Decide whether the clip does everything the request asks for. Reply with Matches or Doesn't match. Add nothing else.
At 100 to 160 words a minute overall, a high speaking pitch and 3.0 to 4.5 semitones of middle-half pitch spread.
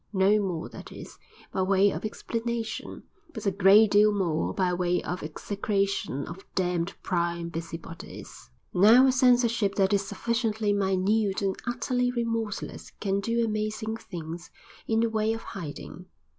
Matches